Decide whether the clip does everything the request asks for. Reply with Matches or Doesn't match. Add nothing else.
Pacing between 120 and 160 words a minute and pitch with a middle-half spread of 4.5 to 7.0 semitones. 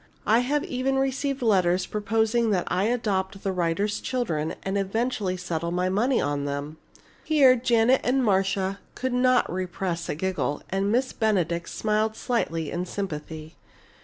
Matches